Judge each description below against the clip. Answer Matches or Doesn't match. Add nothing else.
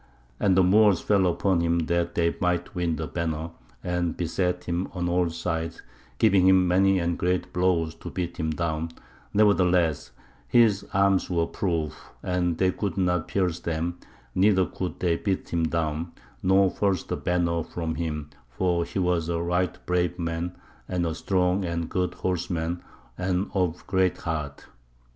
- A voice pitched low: Matches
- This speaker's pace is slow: Doesn't match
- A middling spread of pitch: Doesn't match